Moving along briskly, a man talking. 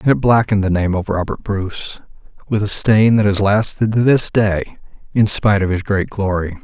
Yes: fast, 210 wpm; male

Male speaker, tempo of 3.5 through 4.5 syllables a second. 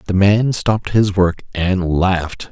Yes: male; 4.0 syllables/s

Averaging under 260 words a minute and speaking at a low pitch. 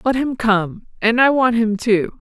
No: fast, 205 wpm; high, 230 Hz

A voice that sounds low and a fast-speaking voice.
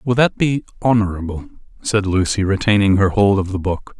No: low, 100 Hz; average, 180 wpm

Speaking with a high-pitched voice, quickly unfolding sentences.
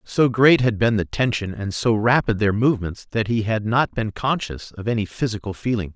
No: low, 110 Hz; fast, 210 wpm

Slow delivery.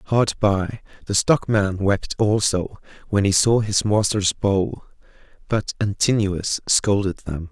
Yes: slow, 130 wpm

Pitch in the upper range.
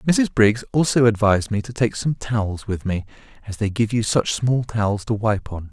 No: low, 110 Hz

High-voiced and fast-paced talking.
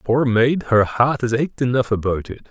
No: low, 120 Hz; fast, 215 wpm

